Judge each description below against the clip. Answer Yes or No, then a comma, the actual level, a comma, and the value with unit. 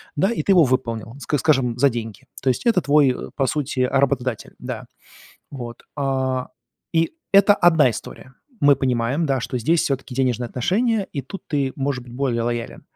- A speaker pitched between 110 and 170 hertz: Yes, low, 135 Hz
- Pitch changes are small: No, average, 3.2 semitones